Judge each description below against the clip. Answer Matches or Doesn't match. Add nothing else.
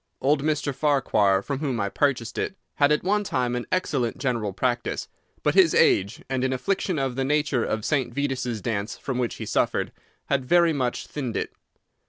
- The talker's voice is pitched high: Doesn't match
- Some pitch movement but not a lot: Matches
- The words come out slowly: Doesn't match